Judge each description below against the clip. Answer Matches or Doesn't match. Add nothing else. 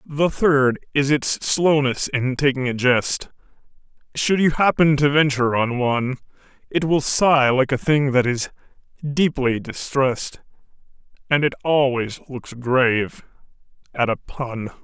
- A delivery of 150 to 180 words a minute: Doesn't match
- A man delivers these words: Matches